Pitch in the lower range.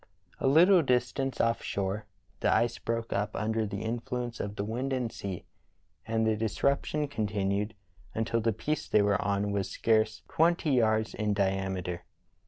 Yes: low, 110 Hz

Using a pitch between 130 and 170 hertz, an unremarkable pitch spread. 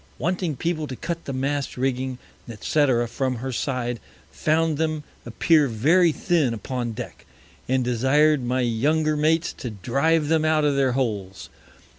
Yes: low, 135 Hz; average, 4.1 semitones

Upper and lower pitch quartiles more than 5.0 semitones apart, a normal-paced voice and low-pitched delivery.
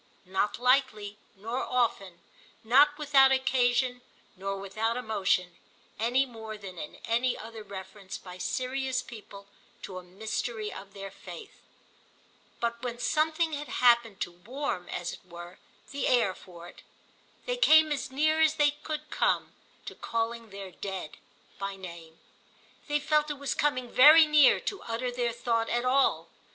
No: wide, 5.5 semitones; average, 150 wpm; high, 235 Hz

